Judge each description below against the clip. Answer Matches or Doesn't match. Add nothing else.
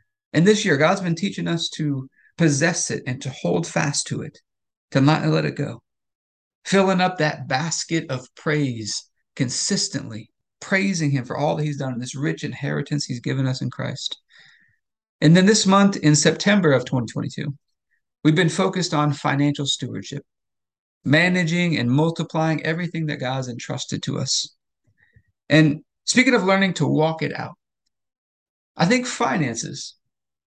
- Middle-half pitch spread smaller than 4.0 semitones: Doesn't match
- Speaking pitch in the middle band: Matches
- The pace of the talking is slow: Doesn't match